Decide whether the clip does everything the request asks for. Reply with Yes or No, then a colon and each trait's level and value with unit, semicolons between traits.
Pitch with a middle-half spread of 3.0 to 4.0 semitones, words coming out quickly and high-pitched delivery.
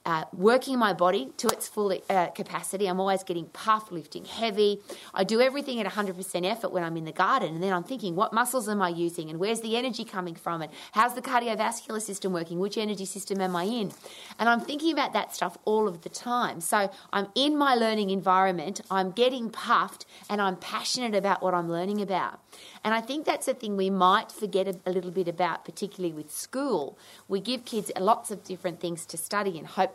Yes: average, 3.4 semitones; fast, 215 wpm; high, 195 Hz